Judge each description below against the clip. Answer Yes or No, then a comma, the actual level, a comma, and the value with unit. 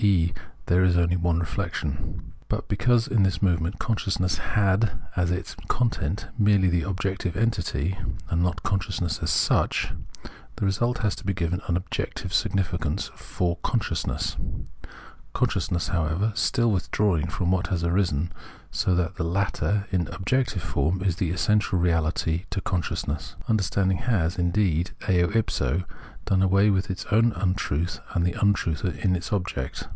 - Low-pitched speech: Yes, very low, 90 Hz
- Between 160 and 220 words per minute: No, average, 150 wpm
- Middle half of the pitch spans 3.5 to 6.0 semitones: No, average, 2.7 semitones